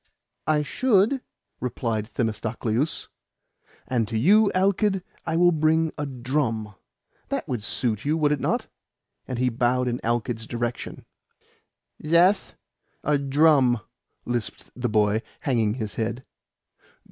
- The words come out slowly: Yes, slow, 125 wpm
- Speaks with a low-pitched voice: Yes, low, 125 Hz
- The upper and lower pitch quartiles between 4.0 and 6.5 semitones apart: Yes, average, 5.3 semitones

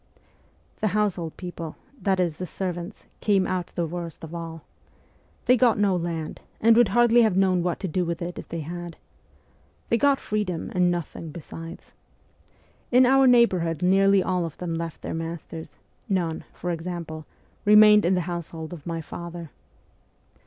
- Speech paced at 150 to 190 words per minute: Yes, average, 170 wpm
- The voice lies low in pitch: No, medium, 175 Hz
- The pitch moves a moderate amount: Yes, average, 3.2 semitones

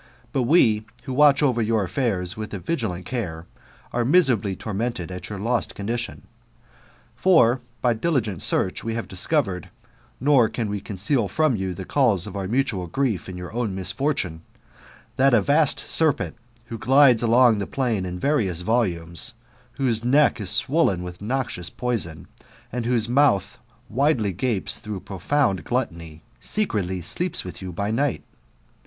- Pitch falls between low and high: No, low, 115 Hz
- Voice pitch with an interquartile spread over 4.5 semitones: Yes, wide, 5.5 semitones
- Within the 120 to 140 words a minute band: No, average, 155 wpm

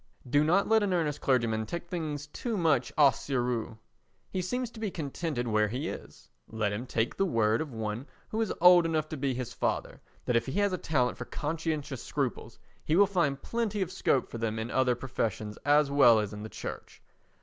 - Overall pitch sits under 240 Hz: Yes, medium, 140 Hz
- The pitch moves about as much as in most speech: No, wide, 6.6 semitones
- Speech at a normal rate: No, fast, 210 wpm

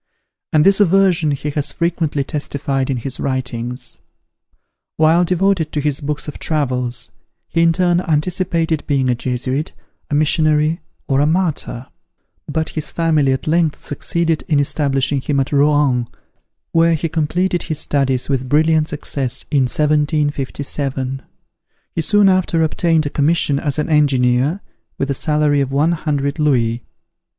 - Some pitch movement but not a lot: Yes, average, 3.1 semitones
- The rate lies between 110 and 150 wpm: Yes, average, 145 wpm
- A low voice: No, medium, 150 Hz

